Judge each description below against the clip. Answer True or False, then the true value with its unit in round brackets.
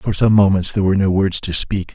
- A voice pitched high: False (95 Hz)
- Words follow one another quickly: True (310 wpm)